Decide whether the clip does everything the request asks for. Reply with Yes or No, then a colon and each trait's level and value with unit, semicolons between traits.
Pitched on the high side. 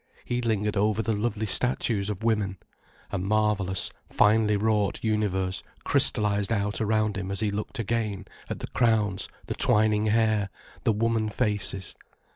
No: low, 105 Hz